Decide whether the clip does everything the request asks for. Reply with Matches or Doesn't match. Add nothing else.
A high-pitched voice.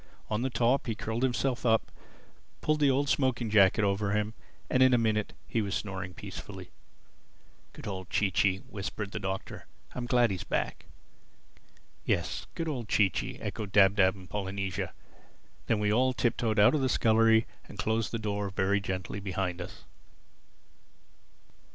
Doesn't match